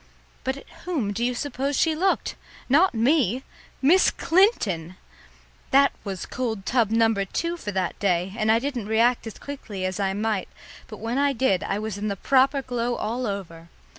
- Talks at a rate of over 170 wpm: Yes, average, 180 wpm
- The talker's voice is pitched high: Yes, high, 230 Hz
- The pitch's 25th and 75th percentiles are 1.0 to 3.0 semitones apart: No, average, 5.3 semitones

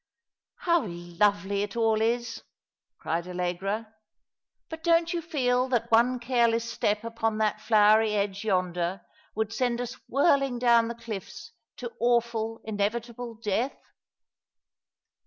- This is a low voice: No, high, 225 Hz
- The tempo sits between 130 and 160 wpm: Yes, slow, 135 wpm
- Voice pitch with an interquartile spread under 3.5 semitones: Yes, average, 2.7 semitones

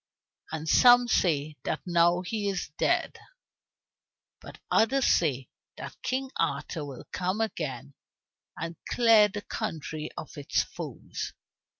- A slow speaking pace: Yes, slow, 120 wpm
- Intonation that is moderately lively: No, wide, 6.3 semitones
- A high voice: No, medium, 175 Hz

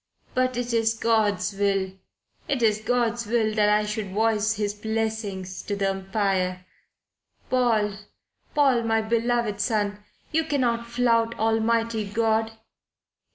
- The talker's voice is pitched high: Yes, high, 220 Hz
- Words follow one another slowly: Yes, slow, 125 wpm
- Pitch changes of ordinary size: No, narrow, 2.2 semitones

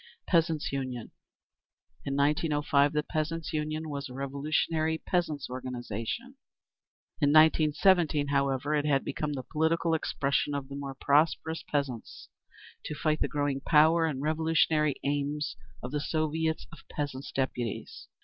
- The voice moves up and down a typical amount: No, narrow, 2.3 semitones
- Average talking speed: No, slow, 130 wpm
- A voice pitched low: No, medium, 150 Hz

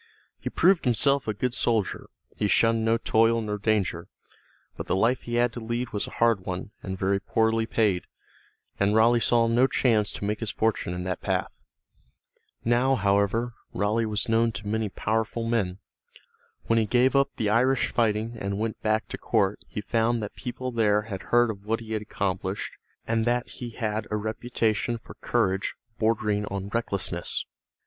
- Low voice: Yes, low, 110 Hz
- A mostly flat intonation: Yes, narrow, 2.3 semitones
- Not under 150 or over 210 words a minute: Yes, average, 180 wpm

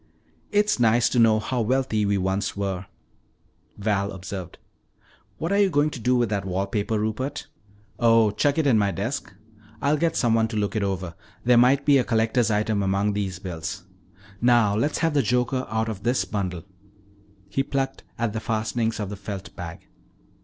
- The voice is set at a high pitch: No, low, 110 Hz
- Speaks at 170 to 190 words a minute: Yes, average, 180 wpm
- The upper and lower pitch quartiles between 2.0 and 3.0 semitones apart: No, average, 3.9 semitones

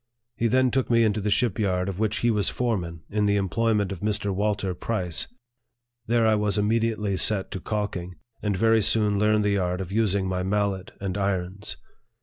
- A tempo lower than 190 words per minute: No, average, 195 wpm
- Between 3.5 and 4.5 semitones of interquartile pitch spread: No, narrow, 2.4 semitones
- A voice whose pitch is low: Yes, low, 105 Hz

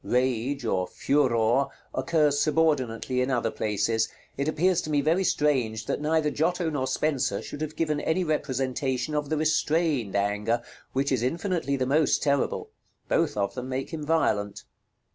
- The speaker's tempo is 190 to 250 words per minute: No, average, 160 wpm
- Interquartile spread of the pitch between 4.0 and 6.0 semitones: Yes, average, 4.4 semitones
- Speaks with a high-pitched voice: No, medium, 140 Hz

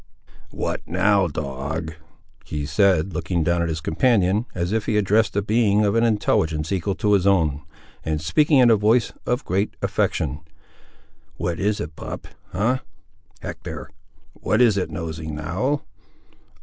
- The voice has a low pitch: Yes, very low, 95 Hz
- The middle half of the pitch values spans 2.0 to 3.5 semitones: No, average, 4.9 semitones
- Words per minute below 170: Yes, average, 150 wpm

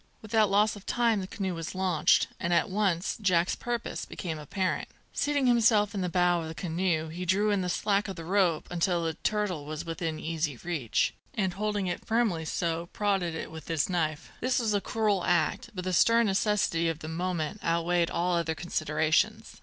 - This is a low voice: No, medium, 180 Hz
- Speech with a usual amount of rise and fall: Yes, average, 3.8 semitones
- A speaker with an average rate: Yes, average, 195 wpm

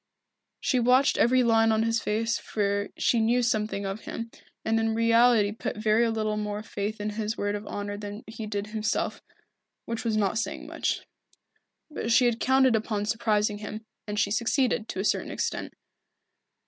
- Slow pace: No, average, 175 wpm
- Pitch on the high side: Yes, high, 220 Hz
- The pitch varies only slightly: Yes, narrow, 1.6 semitones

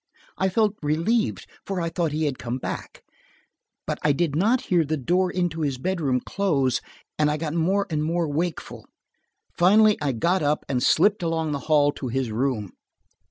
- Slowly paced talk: No, average, 180 wpm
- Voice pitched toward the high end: No, medium, 160 Hz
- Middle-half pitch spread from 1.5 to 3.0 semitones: No, average, 4.2 semitones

